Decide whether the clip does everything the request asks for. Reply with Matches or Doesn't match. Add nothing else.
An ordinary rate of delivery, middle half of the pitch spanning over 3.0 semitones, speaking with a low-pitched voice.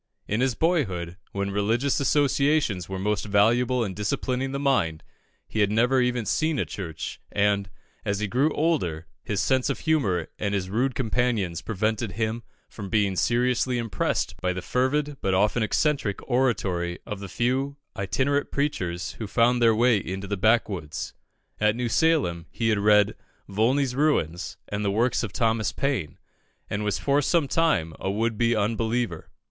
Matches